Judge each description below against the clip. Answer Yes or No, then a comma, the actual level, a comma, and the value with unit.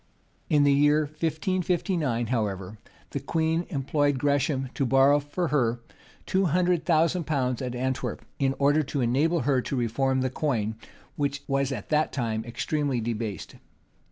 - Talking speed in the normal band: Yes, average, 155 wpm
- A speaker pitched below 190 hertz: Yes, medium, 140 Hz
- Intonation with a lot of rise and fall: No, average, 3.6 semitones